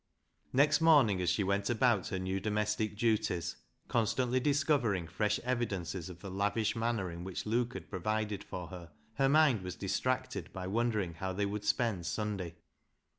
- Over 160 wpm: Yes, average, 180 wpm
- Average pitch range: Yes, average, 4.2 semitones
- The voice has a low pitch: Yes, low, 105 Hz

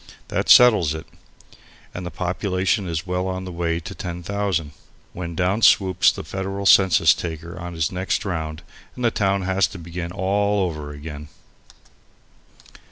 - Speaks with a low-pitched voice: Yes, very low, 90 Hz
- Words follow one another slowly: No, average, 155 wpm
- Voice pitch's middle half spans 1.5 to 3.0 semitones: Yes, average, 2.7 semitones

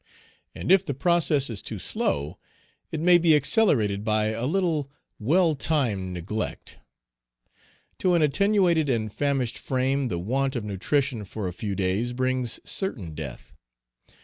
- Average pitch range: No, wide, 6.8 semitones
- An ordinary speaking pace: Yes, average, 145 wpm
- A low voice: Yes, low, 130 Hz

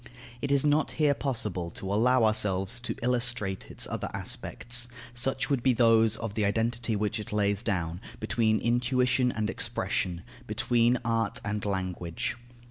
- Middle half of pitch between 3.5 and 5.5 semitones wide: No, average, 3.1 semitones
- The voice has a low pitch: Yes, low, 115 Hz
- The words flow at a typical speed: Yes, average, 155 wpm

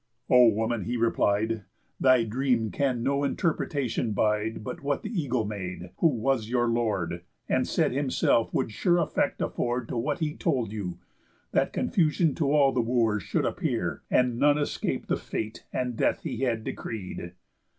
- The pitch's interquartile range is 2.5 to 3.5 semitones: No, average, 4.0 semitones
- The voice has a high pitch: No, low, 120 Hz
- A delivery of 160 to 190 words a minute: Yes, average, 165 wpm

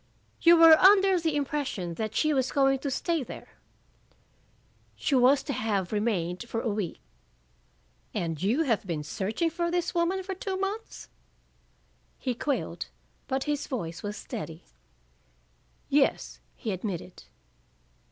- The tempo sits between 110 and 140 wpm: Yes, slow, 135 wpm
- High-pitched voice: Yes, very high, 265 Hz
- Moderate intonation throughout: No, wide, 8.4 semitones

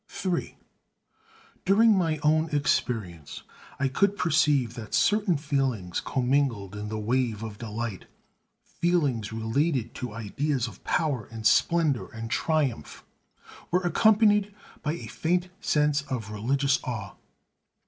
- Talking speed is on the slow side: Yes, slow, 120 wpm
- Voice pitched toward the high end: No, low, 135 Hz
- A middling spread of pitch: No, wide, 6.4 semitones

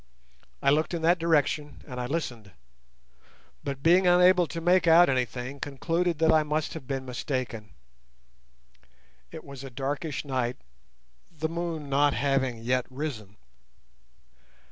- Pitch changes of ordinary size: Yes, average, 4.2 semitones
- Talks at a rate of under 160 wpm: Yes, slow, 135 wpm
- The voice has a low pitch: No, medium, 145 Hz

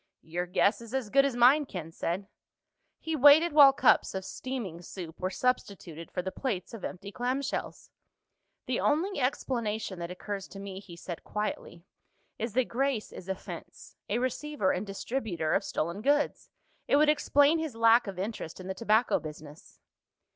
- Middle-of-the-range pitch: No, high, 215 Hz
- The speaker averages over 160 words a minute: Yes, average, 170 wpm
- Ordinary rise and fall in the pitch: No, wide, 6.3 semitones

